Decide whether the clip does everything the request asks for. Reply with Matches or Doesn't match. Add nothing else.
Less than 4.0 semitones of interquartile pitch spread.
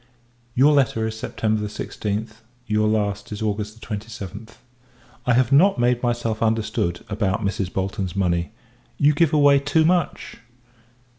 Matches